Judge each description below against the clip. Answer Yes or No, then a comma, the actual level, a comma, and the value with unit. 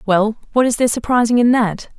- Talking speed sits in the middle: No, fast, 210 wpm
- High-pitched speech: Yes, high, 230 Hz